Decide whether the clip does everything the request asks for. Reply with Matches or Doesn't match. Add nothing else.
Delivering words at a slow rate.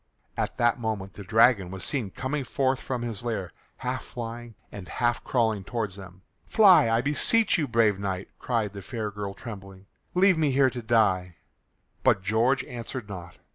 Doesn't match